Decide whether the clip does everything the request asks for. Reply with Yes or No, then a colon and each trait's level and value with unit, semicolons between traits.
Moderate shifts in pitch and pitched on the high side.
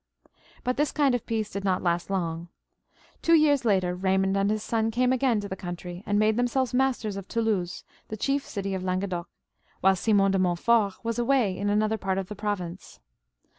Yes: average, 3.7 semitones; high, 205 Hz